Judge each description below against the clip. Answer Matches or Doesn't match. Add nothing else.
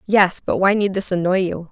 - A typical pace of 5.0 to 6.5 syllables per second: Matches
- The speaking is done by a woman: Matches